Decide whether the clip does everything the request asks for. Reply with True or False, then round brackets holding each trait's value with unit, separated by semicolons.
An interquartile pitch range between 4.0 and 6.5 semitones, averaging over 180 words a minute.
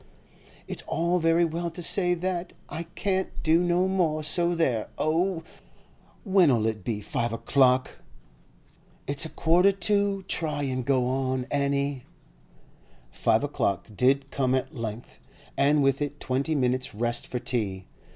False (5.2 semitones; 140 wpm)